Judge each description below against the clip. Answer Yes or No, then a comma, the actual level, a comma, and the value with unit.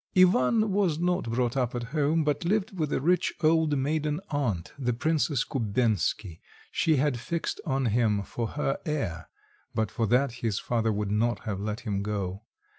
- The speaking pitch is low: Yes, low, 125 Hz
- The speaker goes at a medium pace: Yes, average, 175 wpm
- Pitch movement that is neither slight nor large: No, wide, 5.9 semitones